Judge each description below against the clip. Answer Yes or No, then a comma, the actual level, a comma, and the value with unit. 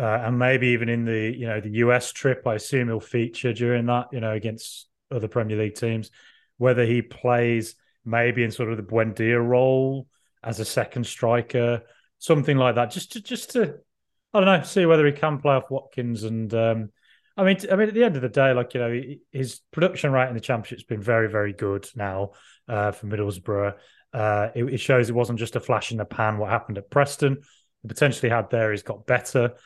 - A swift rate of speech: Yes, fast, 215 wpm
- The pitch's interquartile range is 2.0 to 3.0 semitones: Yes, average, 2.7 semitones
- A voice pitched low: Yes, low, 120 Hz